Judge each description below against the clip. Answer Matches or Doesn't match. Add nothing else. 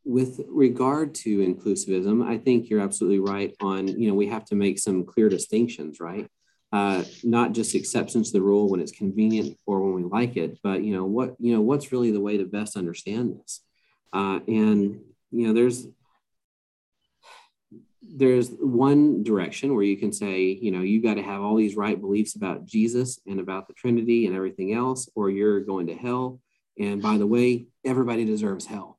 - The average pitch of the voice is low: Matches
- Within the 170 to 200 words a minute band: Matches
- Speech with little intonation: Doesn't match